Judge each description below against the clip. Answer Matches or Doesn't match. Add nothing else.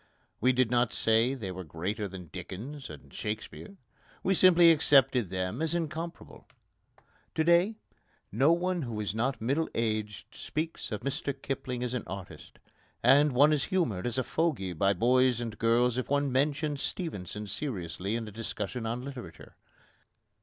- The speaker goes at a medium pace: Matches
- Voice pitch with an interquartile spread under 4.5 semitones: Doesn't match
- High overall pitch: Doesn't match